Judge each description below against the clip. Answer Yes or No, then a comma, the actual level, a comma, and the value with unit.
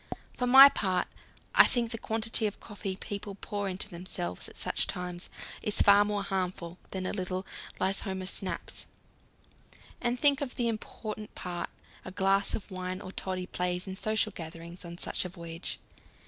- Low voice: No, high, 190 Hz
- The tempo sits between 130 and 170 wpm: Yes, average, 165 wpm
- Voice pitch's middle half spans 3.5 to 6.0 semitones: No, average, 2.8 semitones